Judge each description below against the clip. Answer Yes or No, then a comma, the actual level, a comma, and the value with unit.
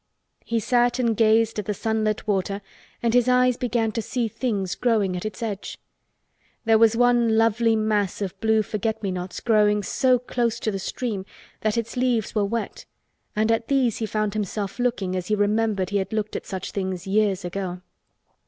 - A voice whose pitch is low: No, high, 215 Hz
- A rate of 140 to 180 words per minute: No, average, 190 wpm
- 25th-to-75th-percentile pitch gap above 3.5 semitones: No, narrow, 2.5 semitones